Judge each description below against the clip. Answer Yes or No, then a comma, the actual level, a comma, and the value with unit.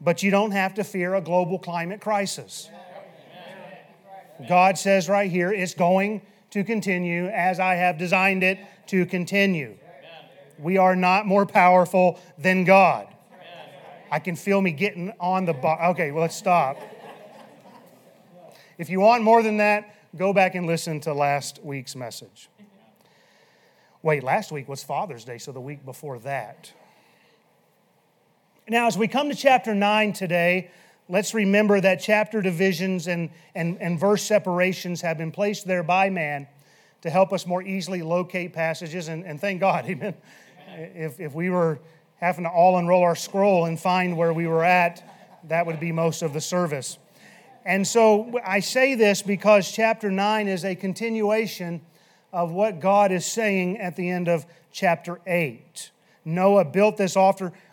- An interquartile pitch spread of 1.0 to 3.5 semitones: Yes, average, 2.8 semitones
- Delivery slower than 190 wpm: Yes, average, 160 wpm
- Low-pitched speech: No, medium, 185 Hz